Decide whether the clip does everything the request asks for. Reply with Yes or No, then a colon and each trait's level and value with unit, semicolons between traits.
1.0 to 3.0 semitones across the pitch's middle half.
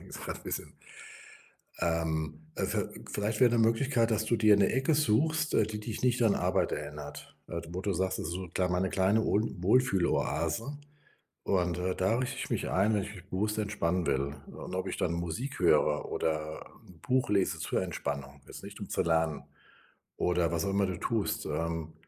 No: average, 4.7 semitones